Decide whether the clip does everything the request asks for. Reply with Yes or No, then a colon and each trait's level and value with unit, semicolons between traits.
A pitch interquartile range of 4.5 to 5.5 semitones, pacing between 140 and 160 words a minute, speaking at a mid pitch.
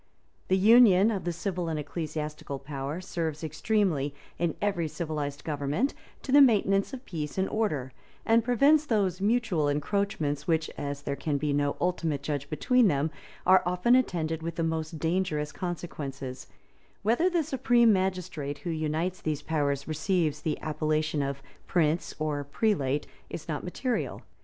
Yes: average, 4.9 semitones; average, 150 wpm; medium, 160 Hz